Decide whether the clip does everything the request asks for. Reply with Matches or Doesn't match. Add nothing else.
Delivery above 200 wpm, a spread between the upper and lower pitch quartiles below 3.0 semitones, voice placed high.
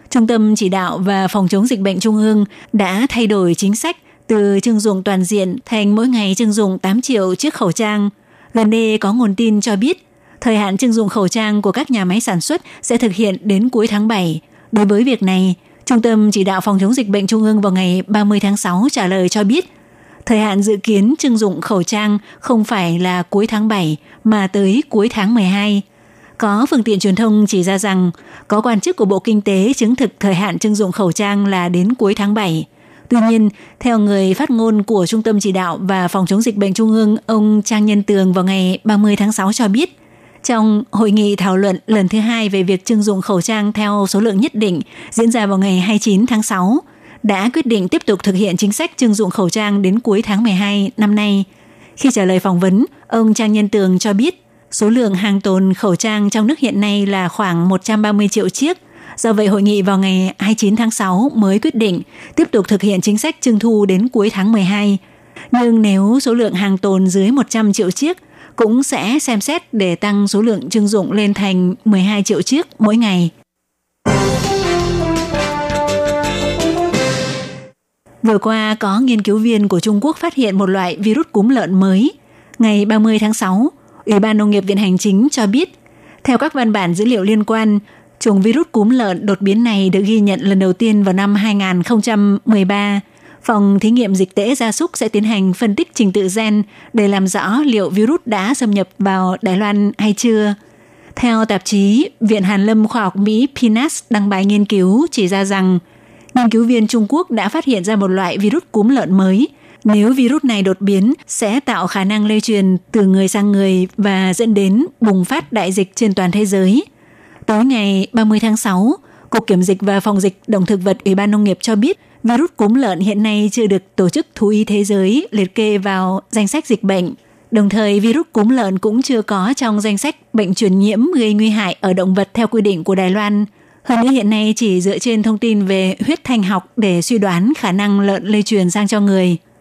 Matches